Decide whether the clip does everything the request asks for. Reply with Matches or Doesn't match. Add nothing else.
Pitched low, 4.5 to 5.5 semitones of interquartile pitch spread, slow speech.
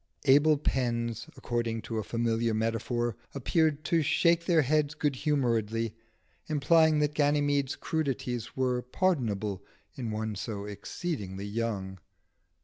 Matches